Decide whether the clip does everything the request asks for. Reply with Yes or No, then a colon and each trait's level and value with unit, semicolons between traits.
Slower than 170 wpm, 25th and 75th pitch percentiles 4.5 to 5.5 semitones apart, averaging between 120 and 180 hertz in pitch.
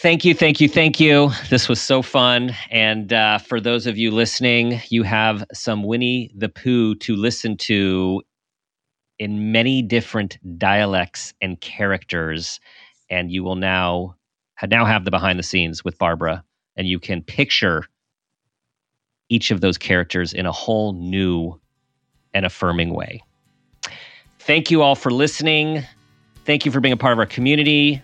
No: average, 155 wpm; average, 5.2 semitones; low, 110 Hz